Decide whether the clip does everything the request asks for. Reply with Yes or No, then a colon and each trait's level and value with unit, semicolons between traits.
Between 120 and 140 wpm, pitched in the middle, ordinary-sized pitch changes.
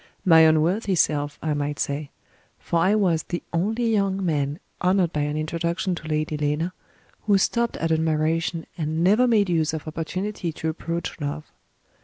No: average, 165 wpm; medium, 165 Hz; average, 3.3 semitones